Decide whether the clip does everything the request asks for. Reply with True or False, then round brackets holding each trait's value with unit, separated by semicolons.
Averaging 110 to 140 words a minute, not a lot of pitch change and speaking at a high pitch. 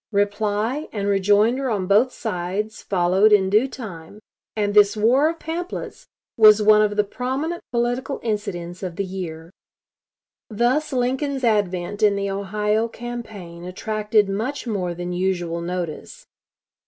False (135 wpm; 4.0 semitones; 210 Hz)